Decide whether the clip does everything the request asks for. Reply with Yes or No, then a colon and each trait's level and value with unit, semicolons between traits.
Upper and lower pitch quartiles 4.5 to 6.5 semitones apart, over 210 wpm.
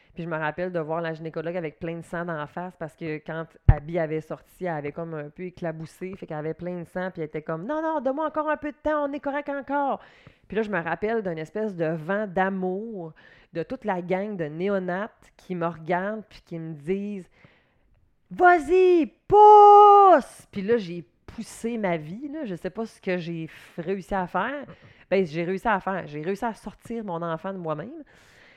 Yes: average, 5.3 semitones; fast, 220 wpm